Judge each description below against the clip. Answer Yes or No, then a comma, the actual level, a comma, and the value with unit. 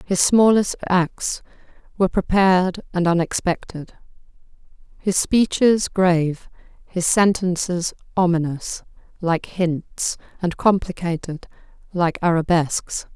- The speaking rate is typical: No, slow, 85 wpm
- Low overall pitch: No, medium, 180 Hz